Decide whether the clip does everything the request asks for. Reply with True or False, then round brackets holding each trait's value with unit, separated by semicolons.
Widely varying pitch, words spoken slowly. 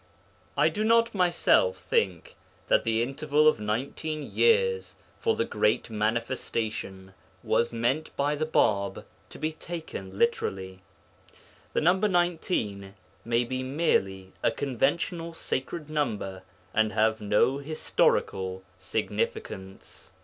True (7.7 semitones; 115 wpm)